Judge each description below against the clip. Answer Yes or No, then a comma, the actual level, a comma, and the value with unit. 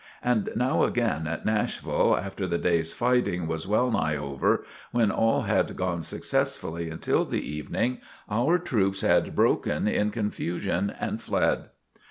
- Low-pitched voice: Yes, very low, 95 Hz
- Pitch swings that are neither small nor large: No, wide, 5.9 semitones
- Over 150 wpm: No, average, 145 wpm